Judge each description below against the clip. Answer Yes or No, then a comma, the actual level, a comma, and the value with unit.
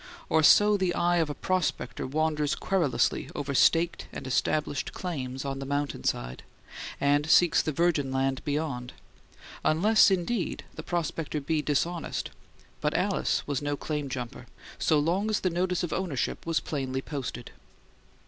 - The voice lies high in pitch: No, medium, 150 Hz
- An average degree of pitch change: Yes, average, 4.2 semitones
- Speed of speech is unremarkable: Yes, average, 150 wpm